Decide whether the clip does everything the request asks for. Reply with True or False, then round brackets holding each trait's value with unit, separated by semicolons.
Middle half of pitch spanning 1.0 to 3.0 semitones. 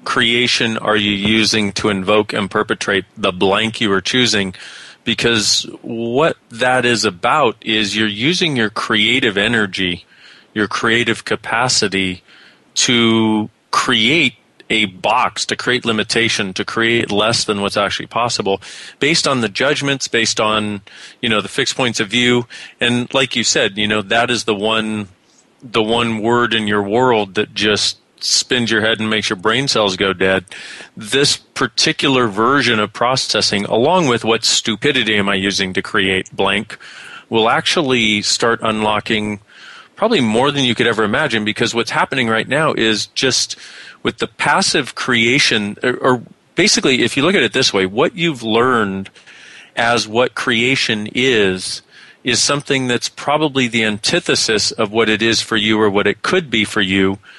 True (2.6 semitones)